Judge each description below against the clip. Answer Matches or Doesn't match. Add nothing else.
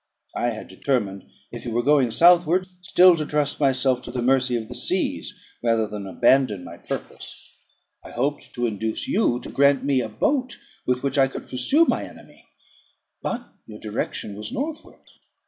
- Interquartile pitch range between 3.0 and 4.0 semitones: Doesn't match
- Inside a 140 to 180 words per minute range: Matches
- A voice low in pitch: Matches